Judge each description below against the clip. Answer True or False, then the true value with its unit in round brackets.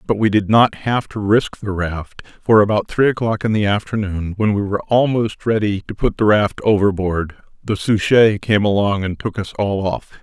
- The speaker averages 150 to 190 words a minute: False (205 wpm)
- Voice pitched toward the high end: False (105 Hz)